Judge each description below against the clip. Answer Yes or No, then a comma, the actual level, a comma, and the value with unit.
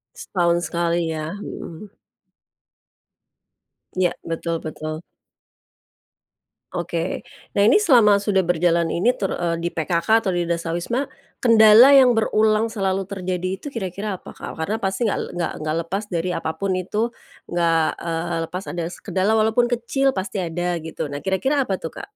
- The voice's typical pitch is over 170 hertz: Yes, medium, 185 Hz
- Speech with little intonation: No, average, 4.1 semitones